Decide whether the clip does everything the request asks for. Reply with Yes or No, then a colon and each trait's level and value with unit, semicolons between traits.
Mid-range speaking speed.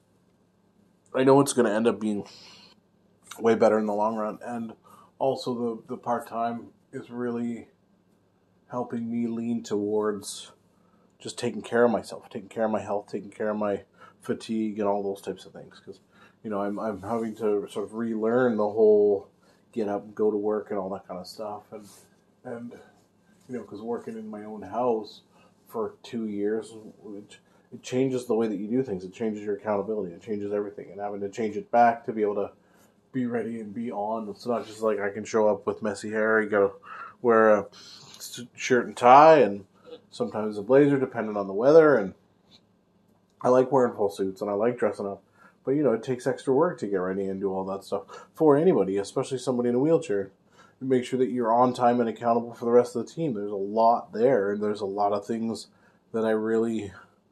No: fast, 210 wpm